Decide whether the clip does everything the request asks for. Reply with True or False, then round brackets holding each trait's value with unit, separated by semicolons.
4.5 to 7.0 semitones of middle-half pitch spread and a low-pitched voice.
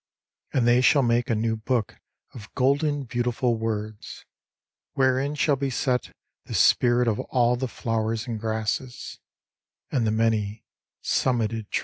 False (2.5 semitones; 120 Hz)